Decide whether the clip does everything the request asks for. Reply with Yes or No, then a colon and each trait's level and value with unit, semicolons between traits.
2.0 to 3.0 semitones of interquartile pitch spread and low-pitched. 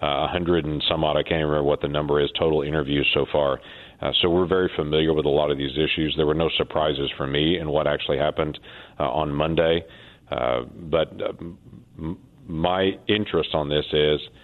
Yes: average, 2.7 semitones; very low, 80 Hz